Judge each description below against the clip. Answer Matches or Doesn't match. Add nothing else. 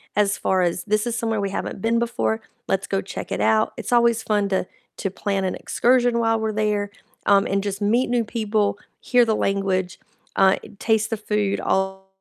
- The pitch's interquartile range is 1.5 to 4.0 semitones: Matches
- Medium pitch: Doesn't match